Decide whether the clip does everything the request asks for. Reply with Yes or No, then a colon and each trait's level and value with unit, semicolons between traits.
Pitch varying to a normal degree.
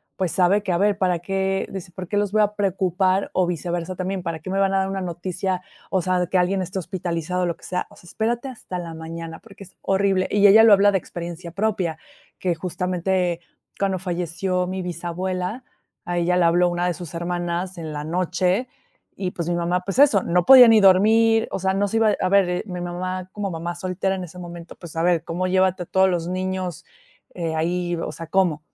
No: narrow, 1.8 semitones